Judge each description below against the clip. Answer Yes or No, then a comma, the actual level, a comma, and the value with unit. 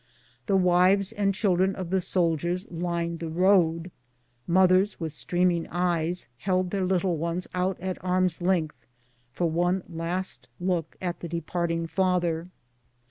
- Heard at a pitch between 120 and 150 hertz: No, medium, 180 Hz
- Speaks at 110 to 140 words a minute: Yes, slow, 135 wpm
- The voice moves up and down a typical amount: No, narrow, 1.7 semitones